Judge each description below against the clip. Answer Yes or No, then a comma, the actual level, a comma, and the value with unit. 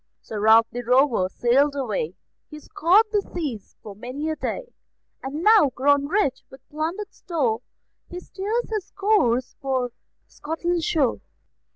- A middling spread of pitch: No, wide, 6.3 semitones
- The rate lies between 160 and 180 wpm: No, average, 145 wpm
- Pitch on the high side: Yes, very high, 285 Hz